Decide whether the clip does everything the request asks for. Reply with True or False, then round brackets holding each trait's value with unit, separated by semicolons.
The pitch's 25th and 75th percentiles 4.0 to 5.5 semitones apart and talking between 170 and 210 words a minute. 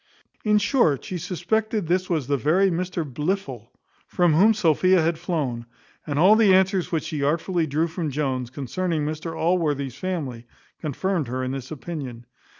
False (4.6 semitones; 160 wpm)